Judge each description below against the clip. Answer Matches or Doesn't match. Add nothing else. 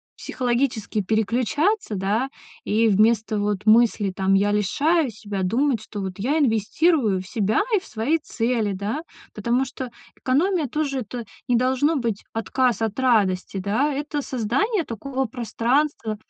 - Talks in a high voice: Matches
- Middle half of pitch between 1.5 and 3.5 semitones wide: Doesn't match